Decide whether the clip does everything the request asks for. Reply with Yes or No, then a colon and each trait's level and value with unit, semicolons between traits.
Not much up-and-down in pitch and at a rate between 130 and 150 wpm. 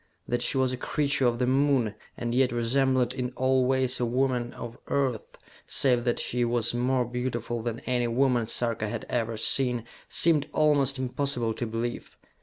No: narrow, 1.9 semitones; average, 175 wpm